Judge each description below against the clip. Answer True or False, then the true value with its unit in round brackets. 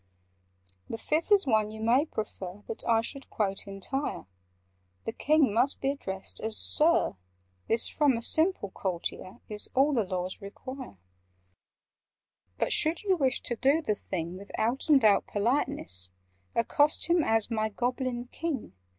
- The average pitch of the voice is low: False (230 Hz)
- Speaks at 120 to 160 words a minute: True (150 wpm)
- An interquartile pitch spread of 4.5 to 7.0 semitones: True (5.6 semitones)